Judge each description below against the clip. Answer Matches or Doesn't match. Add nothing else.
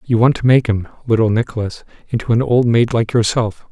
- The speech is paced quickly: Doesn't match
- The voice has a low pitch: Matches